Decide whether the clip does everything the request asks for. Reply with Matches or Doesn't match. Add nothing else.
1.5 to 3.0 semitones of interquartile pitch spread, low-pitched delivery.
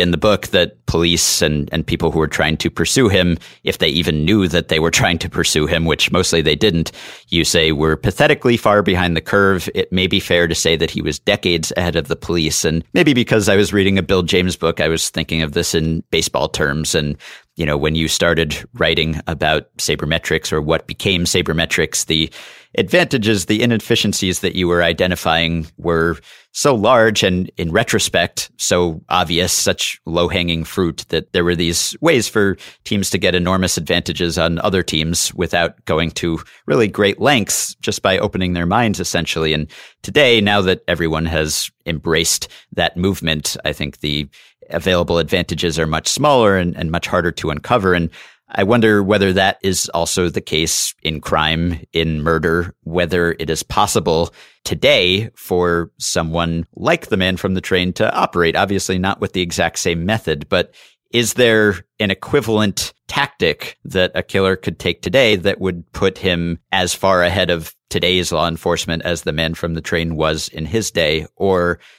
Matches